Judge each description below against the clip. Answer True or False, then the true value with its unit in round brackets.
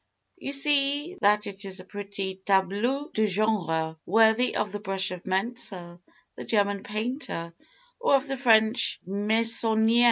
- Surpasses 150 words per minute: False (140 wpm)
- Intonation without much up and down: False (3.6 semitones)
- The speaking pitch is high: True (210 Hz)